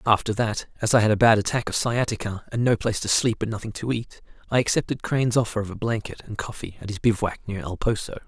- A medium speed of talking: No, fast, 245 wpm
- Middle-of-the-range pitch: No, low, 110 Hz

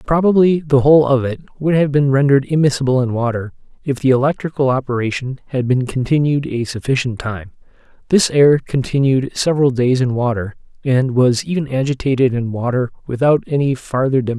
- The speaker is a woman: No, male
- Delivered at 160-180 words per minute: Yes, average, 165 wpm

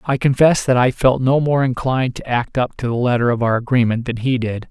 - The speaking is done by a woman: No, male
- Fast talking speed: Yes, fast, 255 wpm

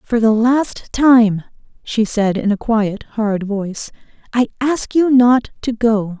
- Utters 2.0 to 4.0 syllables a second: Yes, 3.7 syllables/s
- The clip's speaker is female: Yes, female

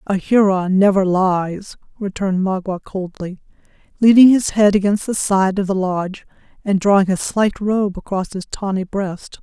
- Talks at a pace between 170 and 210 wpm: No, average, 160 wpm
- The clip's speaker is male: No, female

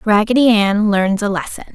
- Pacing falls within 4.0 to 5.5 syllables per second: Yes, 5.1 syllables/s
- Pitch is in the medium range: No, high, 210 Hz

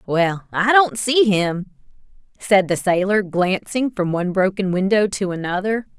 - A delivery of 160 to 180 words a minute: No, average, 150 wpm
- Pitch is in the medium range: No, high, 195 Hz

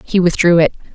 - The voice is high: No, medium, 175 Hz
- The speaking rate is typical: Yes, average, 190 wpm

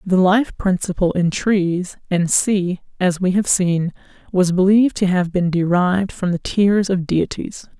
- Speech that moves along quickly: No, average, 170 wpm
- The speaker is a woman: Yes, female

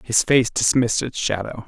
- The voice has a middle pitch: No, low, 120 Hz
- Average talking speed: Yes, average, 180 wpm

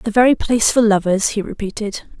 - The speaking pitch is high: Yes, high, 215 Hz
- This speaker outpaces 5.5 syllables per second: Yes, 5.8 syllables/s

